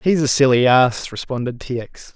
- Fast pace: No, average, 195 wpm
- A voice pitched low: Yes, low, 130 Hz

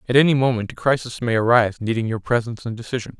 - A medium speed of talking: No, fast, 225 wpm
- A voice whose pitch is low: Yes, low, 120 Hz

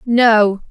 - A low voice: No, high, 220 Hz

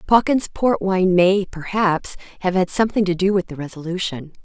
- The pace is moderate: Yes, average, 175 wpm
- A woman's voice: Yes, female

